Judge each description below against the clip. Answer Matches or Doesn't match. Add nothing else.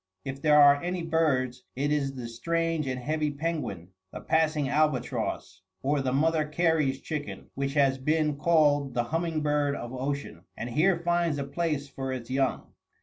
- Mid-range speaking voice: Matches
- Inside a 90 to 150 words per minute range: Doesn't match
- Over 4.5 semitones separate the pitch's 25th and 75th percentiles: Doesn't match